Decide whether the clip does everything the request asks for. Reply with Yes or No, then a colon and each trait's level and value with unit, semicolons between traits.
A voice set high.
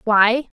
Yes: high, 230 Hz